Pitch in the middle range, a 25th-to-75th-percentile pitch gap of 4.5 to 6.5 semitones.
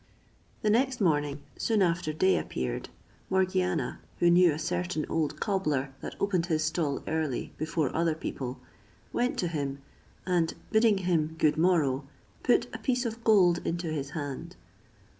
No: medium, 165 Hz; average, 3.7 semitones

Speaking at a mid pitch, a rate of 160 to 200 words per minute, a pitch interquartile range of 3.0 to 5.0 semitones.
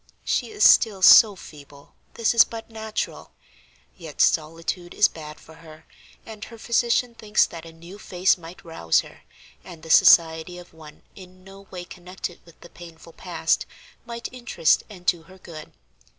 Yes: medium, 175 Hz; average, 165 wpm; average, 4.3 semitones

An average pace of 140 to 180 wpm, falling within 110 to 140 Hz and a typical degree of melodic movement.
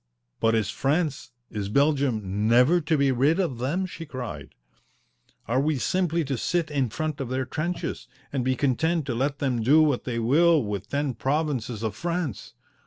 Yes: average, 175 wpm; low, 135 Hz; average, 4.8 semitones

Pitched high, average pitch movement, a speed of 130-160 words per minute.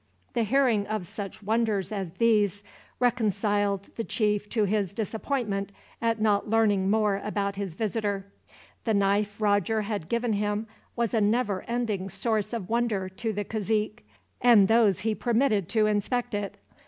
No: high, 210 Hz; narrow, 2.0 semitones; average, 155 wpm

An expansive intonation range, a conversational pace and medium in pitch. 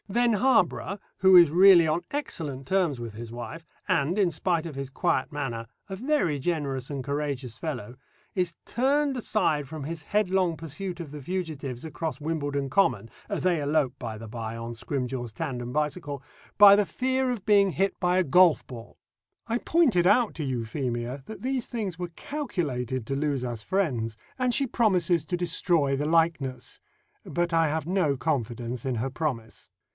Yes: wide, 6.1 semitones; average, 170 wpm; medium, 155 Hz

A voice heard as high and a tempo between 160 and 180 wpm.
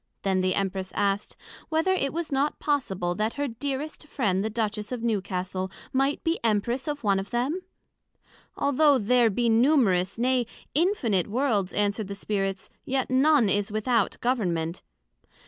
No: high, 225 Hz; average, 150 wpm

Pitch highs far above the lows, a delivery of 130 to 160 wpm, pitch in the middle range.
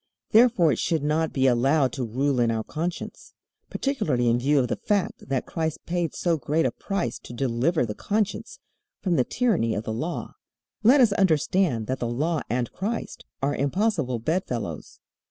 No: wide, 6.5 semitones; average, 175 wpm; medium, 145 Hz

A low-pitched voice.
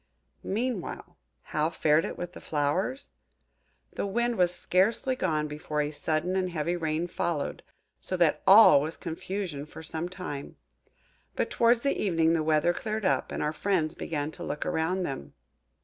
No: medium, 170 Hz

